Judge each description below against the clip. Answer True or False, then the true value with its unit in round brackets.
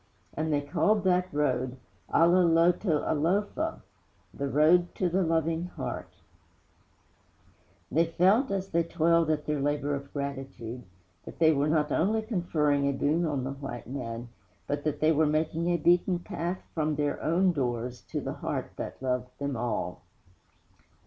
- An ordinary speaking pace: True (155 wpm)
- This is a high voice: False (155 Hz)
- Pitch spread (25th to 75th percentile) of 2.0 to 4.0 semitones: True (3.7 semitones)